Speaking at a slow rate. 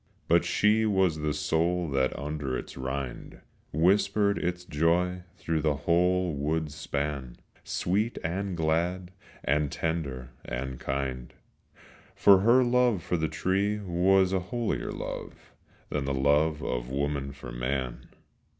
Yes: slow, 130 wpm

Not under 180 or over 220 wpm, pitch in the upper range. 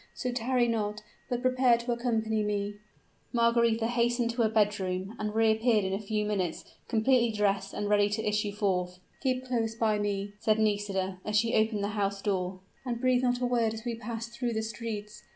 Yes: average, 190 wpm; high, 220 Hz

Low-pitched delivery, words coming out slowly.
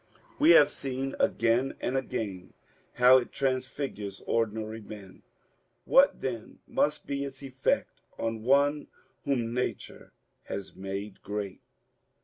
Yes: low, 125 Hz; slow, 120 wpm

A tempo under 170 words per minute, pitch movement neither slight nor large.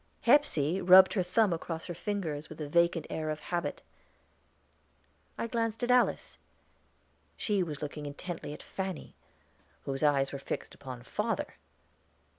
Yes: average, 140 wpm; average, 4.6 semitones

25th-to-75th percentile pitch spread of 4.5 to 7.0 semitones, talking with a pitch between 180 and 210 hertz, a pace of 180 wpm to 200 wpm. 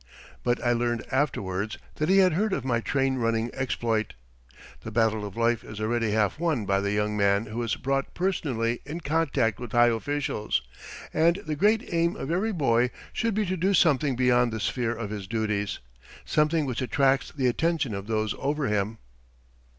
No: wide, 5.5 semitones; low, 120 Hz; average, 185 wpm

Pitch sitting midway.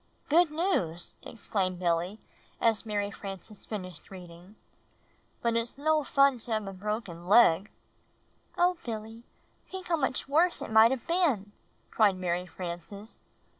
No: high, 215 Hz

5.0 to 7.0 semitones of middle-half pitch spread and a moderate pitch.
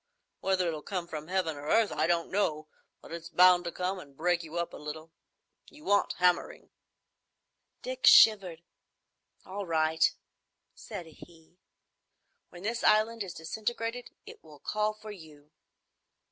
No: average, 4.1 semitones; medium, 175 Hz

